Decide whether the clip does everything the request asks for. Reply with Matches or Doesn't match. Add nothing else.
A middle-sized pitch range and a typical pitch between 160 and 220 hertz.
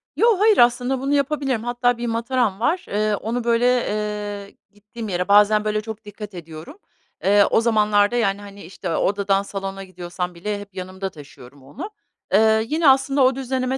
Matches